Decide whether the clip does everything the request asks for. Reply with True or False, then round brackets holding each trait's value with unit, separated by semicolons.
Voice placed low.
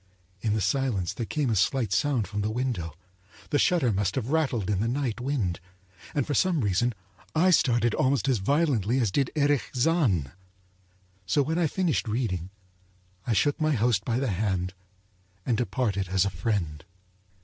True (120 Hz)